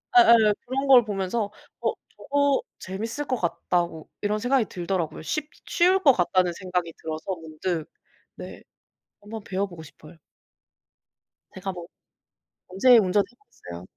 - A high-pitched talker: Yes, high, 195 Hz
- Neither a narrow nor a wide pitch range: No, wide, 5.7 semitones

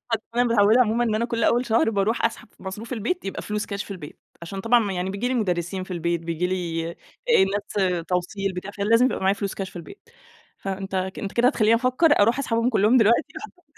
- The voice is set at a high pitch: Yes, high, 205 Hz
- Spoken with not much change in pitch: No, average, 3.8 semitones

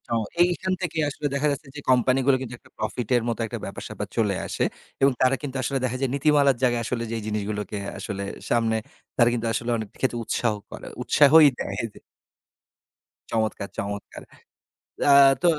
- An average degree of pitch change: Yes, average, 3.9 semitones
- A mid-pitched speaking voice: No, low, 125 Hz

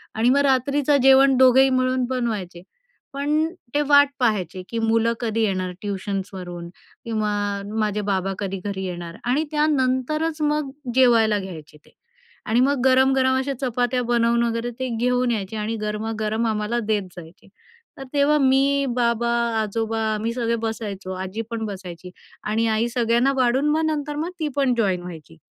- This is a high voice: Yes, high, 235 Hz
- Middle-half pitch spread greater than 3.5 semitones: Yes, average, 4.0 semitones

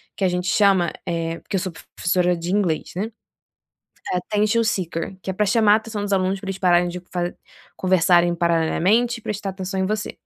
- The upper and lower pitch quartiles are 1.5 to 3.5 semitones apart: Yes, average, 2.8 semitones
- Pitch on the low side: No, medium, 185 Hz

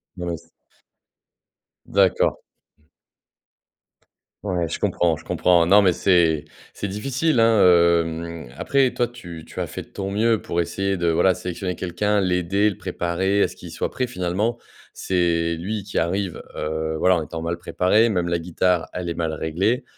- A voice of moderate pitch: No, very low, 90 Hz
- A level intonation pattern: No, average, 3.2 semitones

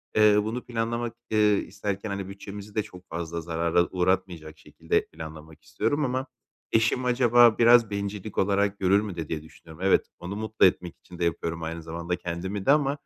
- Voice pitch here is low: Yes, low, 100 Hz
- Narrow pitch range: No, average, 4.6 semitones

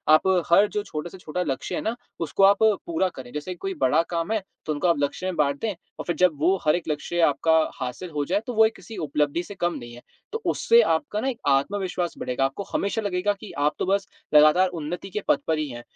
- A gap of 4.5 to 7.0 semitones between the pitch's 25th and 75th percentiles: Yes, average, 5.0 semitones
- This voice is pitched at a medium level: Yes, medium, 175 Hz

